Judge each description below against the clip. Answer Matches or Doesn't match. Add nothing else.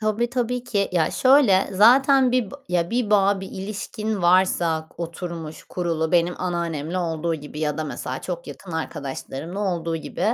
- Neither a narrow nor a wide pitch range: Matches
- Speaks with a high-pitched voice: Doesn't match